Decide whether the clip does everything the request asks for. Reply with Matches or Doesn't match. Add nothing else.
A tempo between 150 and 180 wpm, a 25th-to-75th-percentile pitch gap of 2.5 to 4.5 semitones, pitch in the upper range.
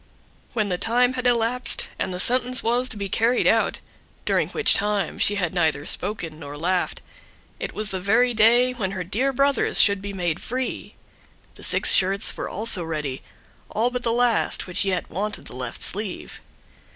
Doesn't match